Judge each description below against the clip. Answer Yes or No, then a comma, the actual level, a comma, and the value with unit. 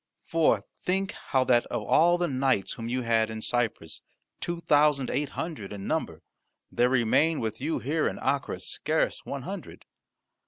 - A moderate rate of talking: Yes, average, 165 wpm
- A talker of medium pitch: No, low, 130 Hz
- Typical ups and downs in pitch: No, wide, 6.0 semitones